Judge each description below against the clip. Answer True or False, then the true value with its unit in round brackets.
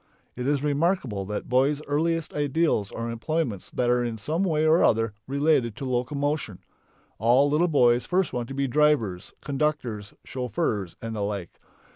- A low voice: True (130 Hz)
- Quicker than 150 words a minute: True (160 wpm)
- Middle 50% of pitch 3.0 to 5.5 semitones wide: True (4.8 semitones)